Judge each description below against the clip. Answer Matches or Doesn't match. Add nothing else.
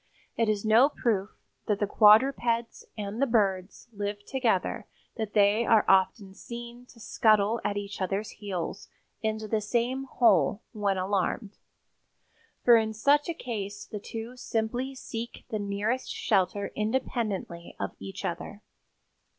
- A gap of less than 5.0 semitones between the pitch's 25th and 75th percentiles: Matches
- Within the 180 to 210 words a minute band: Doesn't match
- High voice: Matches